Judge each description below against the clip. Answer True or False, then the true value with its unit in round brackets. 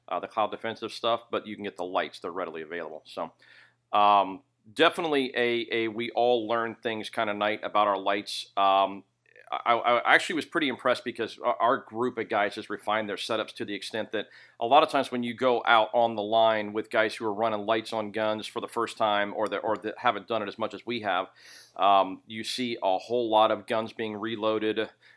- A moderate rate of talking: False (225 wpm)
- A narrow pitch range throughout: True (2.1 semitones)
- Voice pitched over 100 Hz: True (110 Hz)